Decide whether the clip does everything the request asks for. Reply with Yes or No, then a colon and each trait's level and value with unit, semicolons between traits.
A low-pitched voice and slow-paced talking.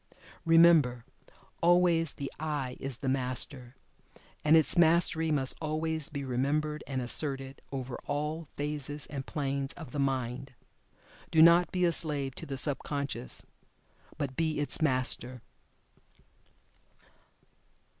No: medium, 145 Hz; slow, 125 wpm